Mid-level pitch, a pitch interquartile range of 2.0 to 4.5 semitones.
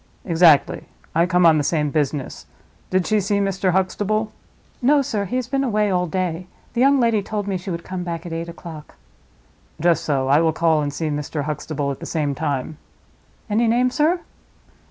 No: medium, 175 Hz; average, 5.3 semitones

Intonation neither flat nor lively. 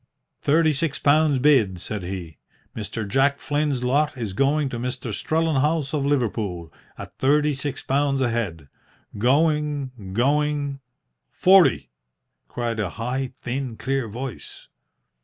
Yes: average, 4.4 semitones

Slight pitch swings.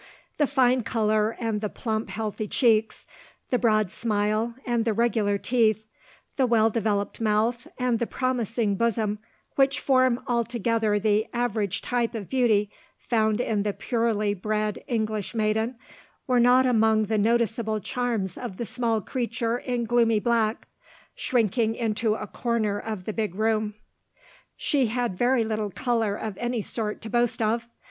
Yes: narrow, 2.0 semitones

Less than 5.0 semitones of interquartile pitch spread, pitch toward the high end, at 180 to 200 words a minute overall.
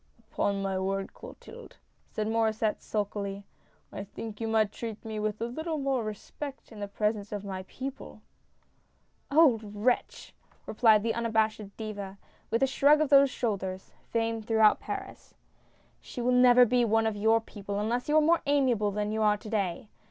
Yes: average, 2.8 semitones; high, 220 Hz; average, 190 wpm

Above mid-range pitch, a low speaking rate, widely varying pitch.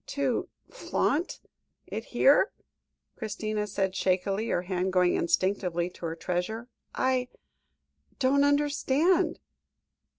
Yes: high, 215 Hz; slow, 105 wpm; wide, 6.9 semitones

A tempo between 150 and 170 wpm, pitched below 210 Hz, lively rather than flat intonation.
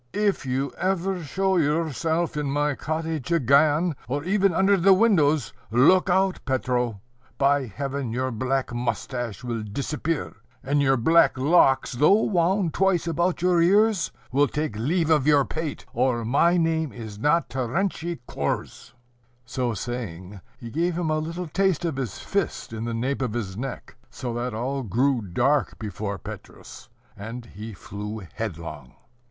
Yes: average, 155 wpm; medium, 140 Hz; wide, 5.8 semitones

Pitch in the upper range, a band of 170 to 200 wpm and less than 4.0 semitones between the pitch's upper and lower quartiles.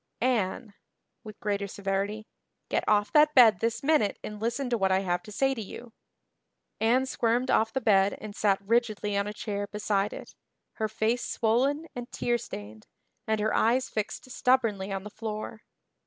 Yes: high, 215 Hz; average, 175 wpm; average, 3.0 semitones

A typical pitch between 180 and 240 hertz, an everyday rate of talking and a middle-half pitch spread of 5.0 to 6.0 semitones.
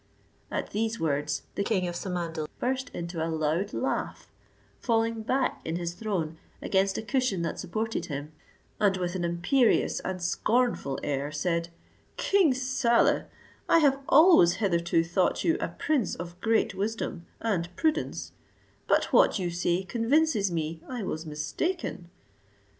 Yes: high, 190 Hz; average, 145 wpm; wide, 5.5 semitones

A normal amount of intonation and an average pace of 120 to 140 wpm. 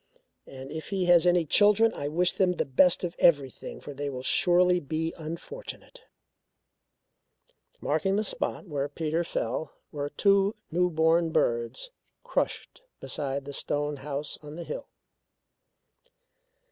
Yes: average, 3.8 semitones; slow, 135 wpm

